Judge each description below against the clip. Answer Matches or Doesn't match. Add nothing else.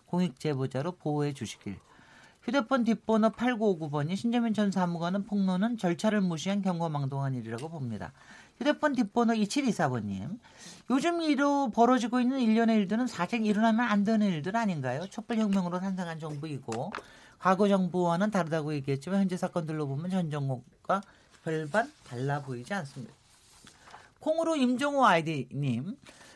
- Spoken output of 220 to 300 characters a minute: Doesn't match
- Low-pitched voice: Doesn't match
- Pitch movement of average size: Doesn't match